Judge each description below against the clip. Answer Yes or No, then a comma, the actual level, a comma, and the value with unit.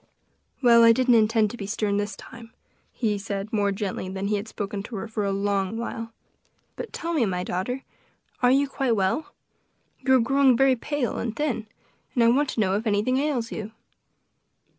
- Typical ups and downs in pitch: Yes, average, 3.7 semitones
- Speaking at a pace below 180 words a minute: No, average, 195 wpm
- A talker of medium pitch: No, high, 225 Hz